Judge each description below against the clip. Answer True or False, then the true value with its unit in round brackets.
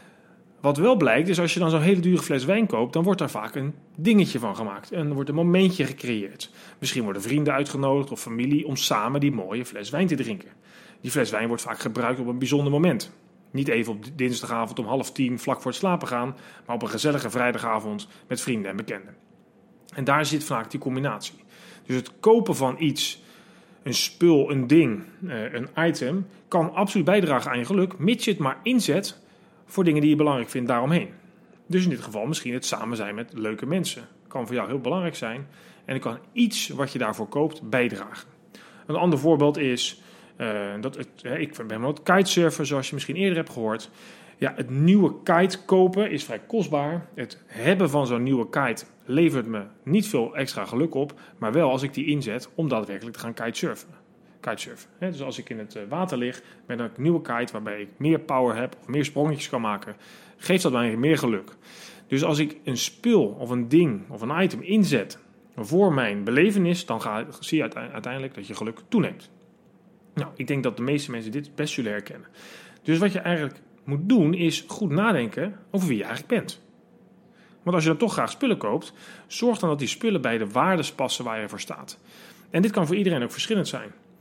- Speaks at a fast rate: True (205 wpm)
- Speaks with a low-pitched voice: False (150 Hz)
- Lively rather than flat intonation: True (6.6 semitones)